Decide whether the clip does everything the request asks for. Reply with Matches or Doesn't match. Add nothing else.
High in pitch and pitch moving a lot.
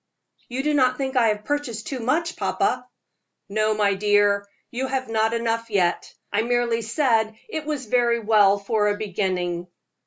Doesn't match